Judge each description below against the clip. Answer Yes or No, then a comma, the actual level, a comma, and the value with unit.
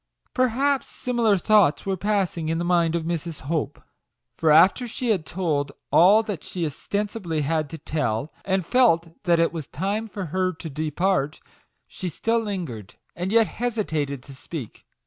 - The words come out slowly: No, average, 160 wpm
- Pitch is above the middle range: No, medium, 175 Hz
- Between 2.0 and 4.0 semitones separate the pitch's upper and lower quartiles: No, average, 4.8 semitones